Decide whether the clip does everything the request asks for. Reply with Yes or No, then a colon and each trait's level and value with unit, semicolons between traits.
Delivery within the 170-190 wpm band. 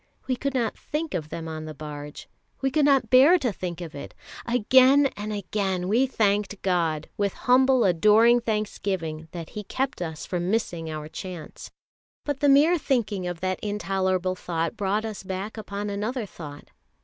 Yes: average, 175 wpm